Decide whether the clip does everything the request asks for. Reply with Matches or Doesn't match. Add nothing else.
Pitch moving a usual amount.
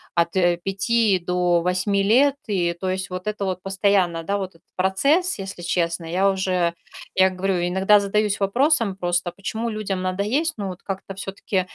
Doesn't match